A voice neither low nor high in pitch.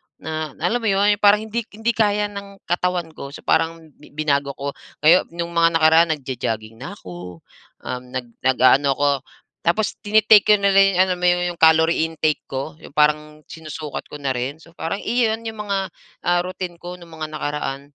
Yes: medium, 165 Hz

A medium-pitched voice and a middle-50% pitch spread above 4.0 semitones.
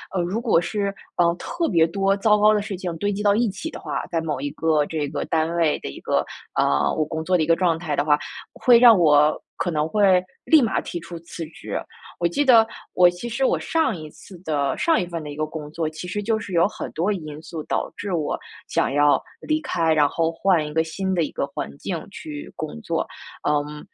Yes: medium, 170 Hz; average, 4.6 semitones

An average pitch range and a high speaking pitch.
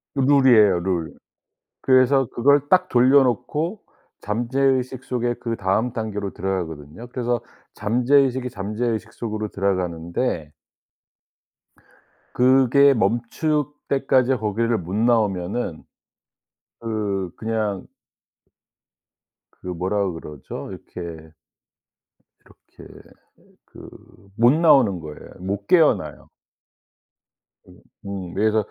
No: average, 5.0 semitones; low, 115 Hz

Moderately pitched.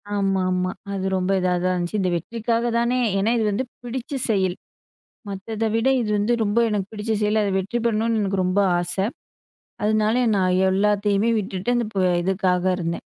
No: high, 205 Hz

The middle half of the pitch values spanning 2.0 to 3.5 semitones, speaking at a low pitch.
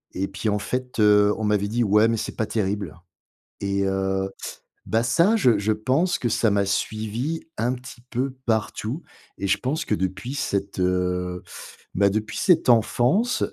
No: average, 4.0 semitones; low, 110 Hz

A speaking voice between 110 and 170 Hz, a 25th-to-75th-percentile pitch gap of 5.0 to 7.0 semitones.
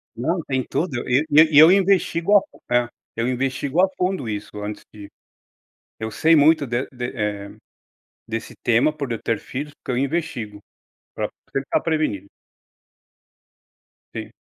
Yes: low, 135 Hz; wide, 5.6 semitones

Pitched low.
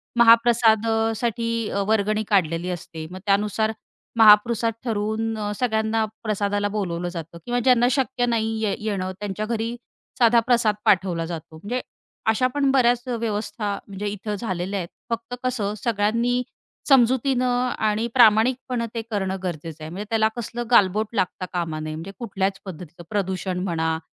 No: high, 215 Hz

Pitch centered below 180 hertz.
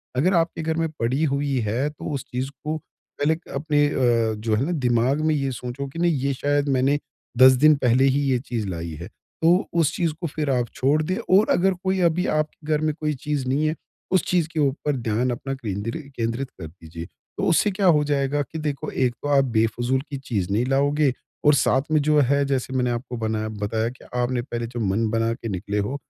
Yes: low, 135 Hz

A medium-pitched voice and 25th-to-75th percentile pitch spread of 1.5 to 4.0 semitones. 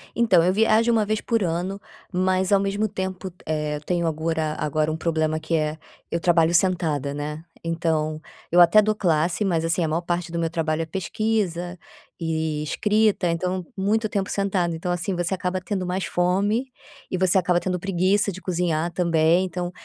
Yes: medium, 175 Hz; average, 2.9 semitones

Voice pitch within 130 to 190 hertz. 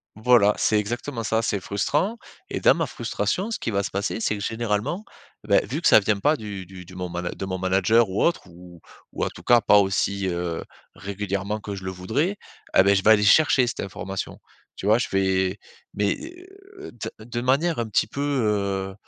No: low, 105 Hz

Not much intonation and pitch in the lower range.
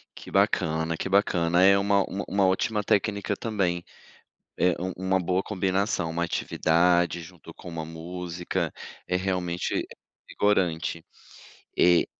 Yes: narrow, 2.3 semitones; very low, 90 Hz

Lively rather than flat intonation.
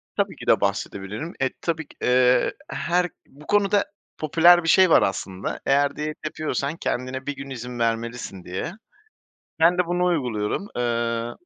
Yes: wide, 6.1 semitones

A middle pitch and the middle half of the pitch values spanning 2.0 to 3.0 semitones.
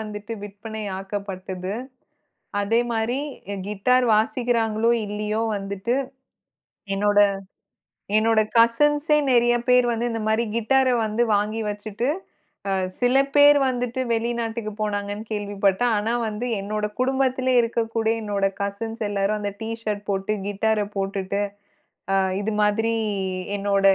No: high, 220 Hz; narrow, 2.4 semitones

